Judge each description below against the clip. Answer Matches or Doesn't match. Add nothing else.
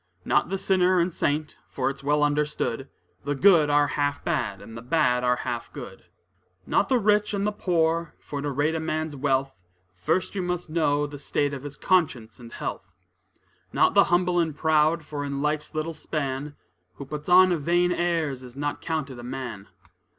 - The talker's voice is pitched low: Doesn't match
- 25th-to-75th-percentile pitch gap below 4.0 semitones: Matches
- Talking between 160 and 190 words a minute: Matches